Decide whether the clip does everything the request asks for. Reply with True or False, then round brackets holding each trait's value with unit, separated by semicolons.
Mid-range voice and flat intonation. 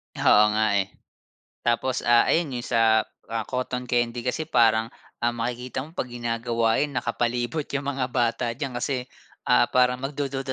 False (120 Hz; 2.0 semitones)